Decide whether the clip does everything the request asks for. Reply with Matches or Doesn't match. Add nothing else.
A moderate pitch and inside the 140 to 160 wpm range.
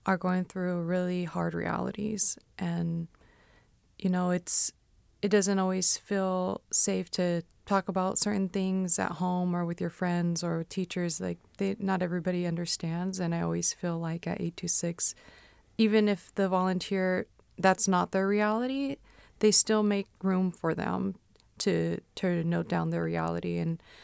Matches